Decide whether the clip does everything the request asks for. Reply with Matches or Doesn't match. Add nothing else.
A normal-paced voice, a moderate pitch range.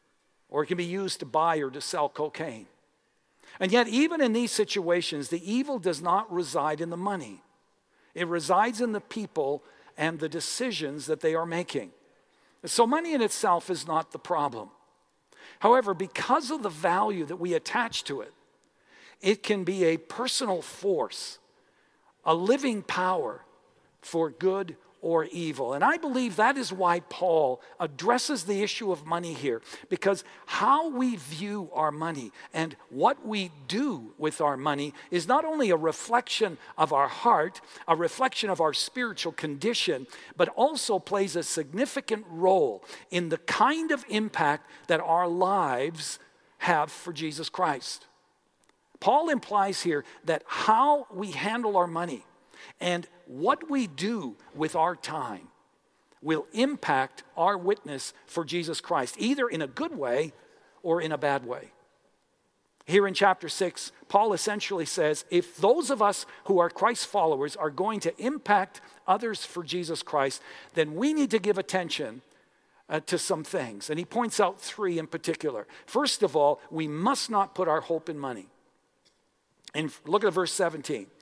Doesn't match